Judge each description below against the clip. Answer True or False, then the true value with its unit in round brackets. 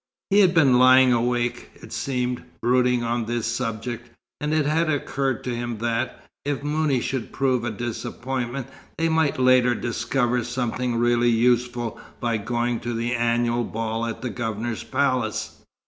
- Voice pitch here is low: True (120 Hz)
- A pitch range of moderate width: False (1.6 semitones)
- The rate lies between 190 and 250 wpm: False (155 wpm)